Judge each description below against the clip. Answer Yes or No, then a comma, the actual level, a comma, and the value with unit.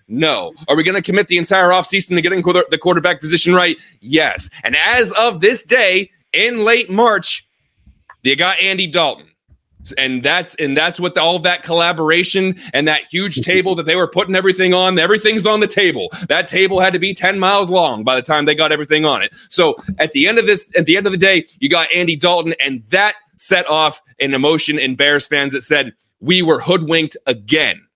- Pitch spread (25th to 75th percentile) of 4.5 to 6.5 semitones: No, average, 3.6 semitones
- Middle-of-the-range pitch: Yes, medium, 175 Hz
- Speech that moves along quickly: Yes, fast, 210 wpm